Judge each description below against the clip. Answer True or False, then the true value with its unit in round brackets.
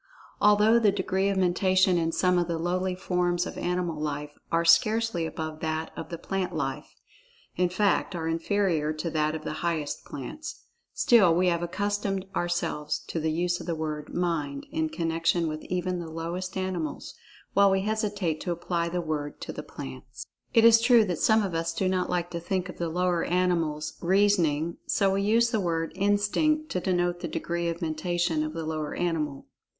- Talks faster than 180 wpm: True (190 wpm)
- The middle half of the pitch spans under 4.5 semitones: True (2.8 semitones)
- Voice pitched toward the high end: False (175 Hz)